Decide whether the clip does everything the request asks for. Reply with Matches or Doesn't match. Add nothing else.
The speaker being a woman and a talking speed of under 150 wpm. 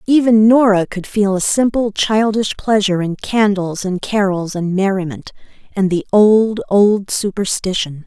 Matches